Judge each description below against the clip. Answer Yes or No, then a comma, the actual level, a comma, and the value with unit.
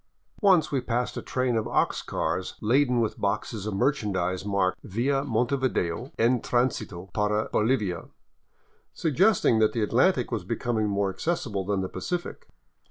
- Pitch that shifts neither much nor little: Yes, average, 4.5 semitones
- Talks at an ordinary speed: Yes, average, 150 wpm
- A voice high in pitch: No, low, 115 Hz